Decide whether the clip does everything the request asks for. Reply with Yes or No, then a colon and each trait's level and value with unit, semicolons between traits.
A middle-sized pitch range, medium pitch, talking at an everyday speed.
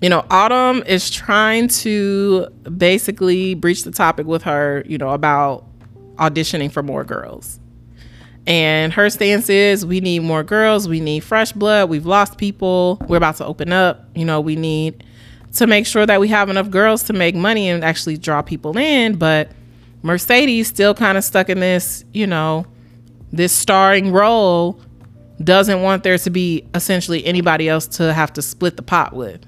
Yes: average, 4.4 semitones; medium, 175 Hz; average, 175 wpm